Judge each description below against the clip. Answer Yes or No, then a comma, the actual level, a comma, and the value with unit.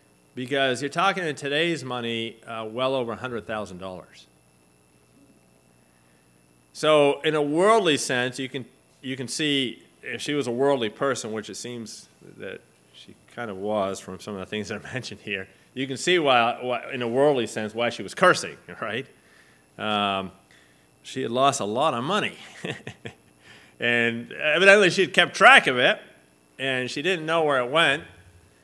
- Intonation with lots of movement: Yes, wide, 6.8 semitones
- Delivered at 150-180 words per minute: Yes, average, 165 wpm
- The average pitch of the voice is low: Yes, low, 115 Hz